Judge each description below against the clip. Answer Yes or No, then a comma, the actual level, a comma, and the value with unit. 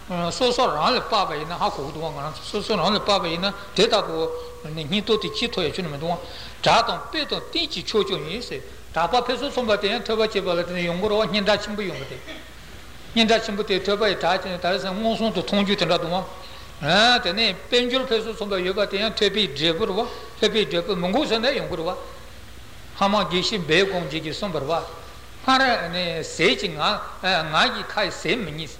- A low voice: No, high, 200 Hz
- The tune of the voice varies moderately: Yes, average, 4.0 semitones